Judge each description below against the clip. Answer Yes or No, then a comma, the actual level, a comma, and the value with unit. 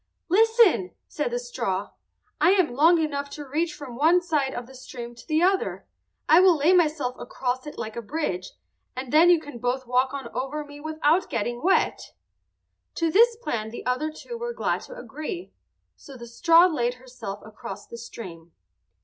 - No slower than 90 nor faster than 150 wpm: No, average, 185 wpm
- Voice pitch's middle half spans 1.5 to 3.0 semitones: No, wide, 5.4 semitones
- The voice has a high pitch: Yes, very high, 285 Hz